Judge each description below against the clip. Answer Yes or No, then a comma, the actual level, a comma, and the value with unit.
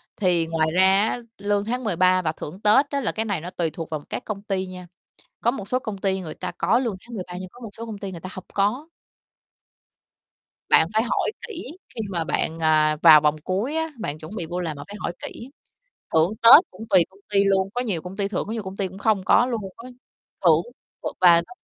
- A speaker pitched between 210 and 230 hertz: No, high, 195 Hz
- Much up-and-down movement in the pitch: No, average, 4.2 semitones